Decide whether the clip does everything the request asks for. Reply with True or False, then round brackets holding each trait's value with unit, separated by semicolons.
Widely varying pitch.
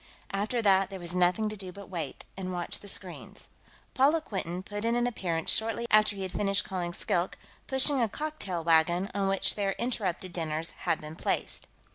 False (3.4 semitones)